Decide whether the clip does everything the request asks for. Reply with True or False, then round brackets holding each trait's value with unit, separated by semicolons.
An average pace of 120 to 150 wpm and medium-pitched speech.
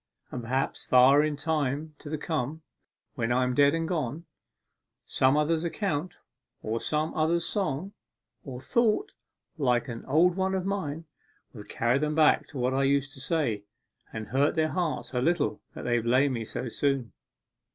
False (170 wpm; 145 Hz)